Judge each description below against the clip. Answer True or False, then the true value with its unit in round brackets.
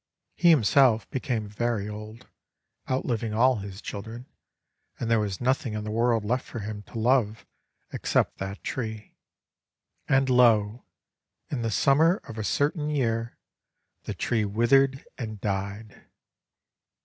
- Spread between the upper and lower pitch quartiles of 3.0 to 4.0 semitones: True (3.3 semitones)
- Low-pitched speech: True (115 Hz)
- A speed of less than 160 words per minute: True (135 wpm)